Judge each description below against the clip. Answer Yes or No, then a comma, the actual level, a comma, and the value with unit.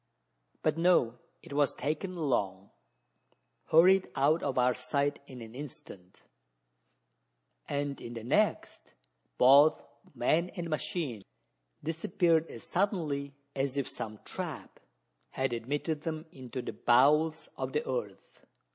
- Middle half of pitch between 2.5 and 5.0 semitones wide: Yes, average, 4.3 semitones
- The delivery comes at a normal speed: No, slow, 120 wpm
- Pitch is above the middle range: No, medium, 145 Hz